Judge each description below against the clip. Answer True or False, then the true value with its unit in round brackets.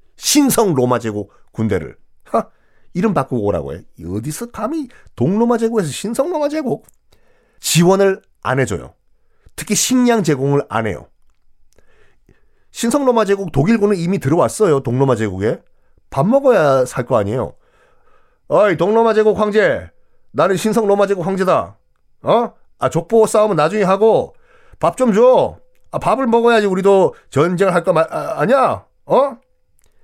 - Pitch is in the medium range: False (200 Hz)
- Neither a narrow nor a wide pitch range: False (7.8 semitones)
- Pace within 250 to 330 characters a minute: True (280 characters per minute)